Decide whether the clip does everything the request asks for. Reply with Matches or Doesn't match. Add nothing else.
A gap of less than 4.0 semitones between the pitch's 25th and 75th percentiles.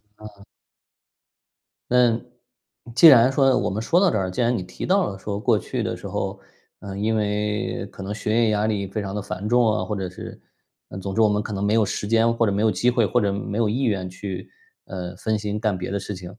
Matches